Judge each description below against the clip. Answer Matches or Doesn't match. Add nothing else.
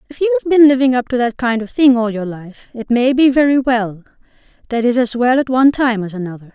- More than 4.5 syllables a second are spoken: Matches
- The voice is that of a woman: Matches